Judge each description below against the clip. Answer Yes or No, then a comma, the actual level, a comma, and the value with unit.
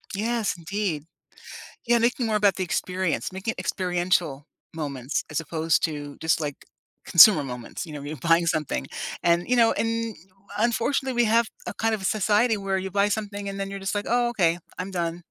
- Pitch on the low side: No, high, 190 Hz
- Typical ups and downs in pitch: Yes, average, 5.0 semitones